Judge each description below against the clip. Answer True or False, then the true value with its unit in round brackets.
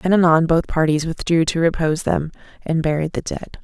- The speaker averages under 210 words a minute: True (200 wpm)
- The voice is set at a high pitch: False (165 Hz)